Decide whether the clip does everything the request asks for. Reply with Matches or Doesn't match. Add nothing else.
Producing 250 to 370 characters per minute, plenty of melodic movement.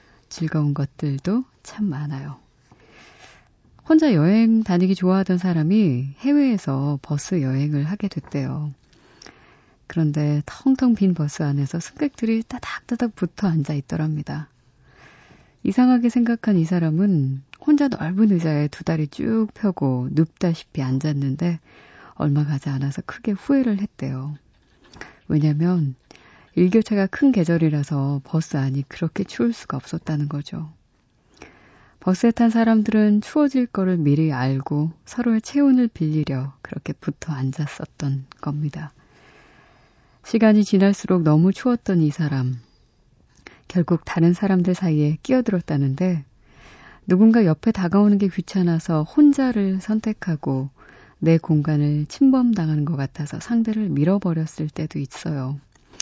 Matches